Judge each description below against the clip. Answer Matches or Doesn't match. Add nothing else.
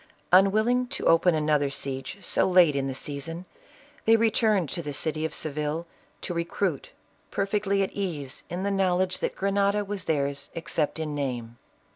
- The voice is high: Doesn't match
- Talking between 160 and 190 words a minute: Matches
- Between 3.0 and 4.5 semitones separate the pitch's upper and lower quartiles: Doesn't match